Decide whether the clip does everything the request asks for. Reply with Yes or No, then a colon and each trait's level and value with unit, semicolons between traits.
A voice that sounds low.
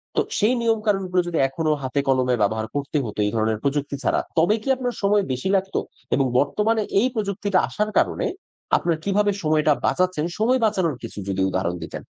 No: medium, 175 Hz